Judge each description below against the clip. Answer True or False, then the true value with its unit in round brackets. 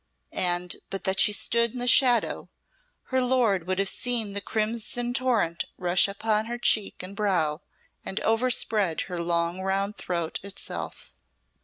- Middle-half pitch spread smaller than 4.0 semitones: False (4.3 semitones)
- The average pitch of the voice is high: True (200 Hz)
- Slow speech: False (150 wpm)